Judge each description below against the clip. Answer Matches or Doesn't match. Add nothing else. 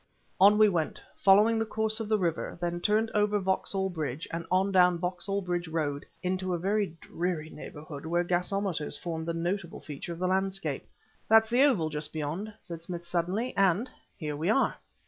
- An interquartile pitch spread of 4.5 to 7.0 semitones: Doesn't match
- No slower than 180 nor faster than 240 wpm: Matches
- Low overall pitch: Doesn't match